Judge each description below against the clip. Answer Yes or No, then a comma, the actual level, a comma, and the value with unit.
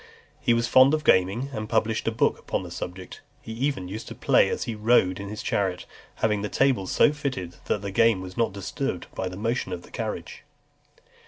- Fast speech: Yes, fast, 215 wpm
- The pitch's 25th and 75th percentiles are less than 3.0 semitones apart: No, average, 3.9 semitones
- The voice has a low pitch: Yes, low, 105 Hz